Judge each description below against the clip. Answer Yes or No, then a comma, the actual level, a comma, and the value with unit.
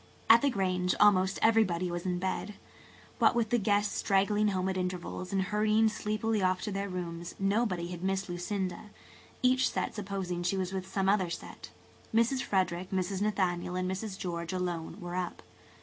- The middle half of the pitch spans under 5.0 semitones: Yes, narrow, 2.5 semitones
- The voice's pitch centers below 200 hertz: Yes, high, 190 Hz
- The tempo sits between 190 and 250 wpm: No, average, 175 wpm